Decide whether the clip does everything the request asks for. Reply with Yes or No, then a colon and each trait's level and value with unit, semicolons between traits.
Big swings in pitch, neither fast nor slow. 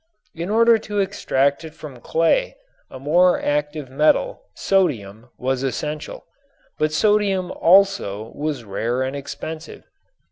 No: wide, 6.3 semitones; slow, 120 wpm